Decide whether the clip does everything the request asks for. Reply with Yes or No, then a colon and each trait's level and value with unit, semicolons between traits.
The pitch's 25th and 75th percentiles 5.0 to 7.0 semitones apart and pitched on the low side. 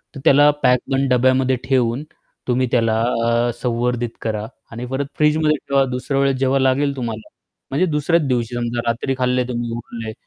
No: narrow, 2.5 semitones; low, 125 Hz